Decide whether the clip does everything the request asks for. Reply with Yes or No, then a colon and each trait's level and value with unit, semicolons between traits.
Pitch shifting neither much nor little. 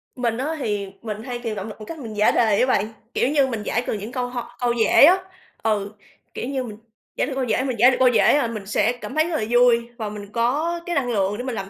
Yes: average, 3.3 semitones